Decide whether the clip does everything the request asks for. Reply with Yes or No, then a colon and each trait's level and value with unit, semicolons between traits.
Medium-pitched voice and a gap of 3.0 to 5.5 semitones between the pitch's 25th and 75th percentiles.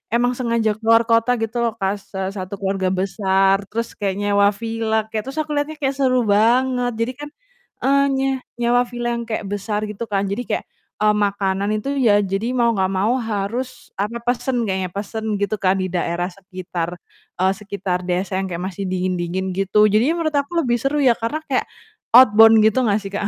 No: high, 215 Hz; average, 3.7 semitones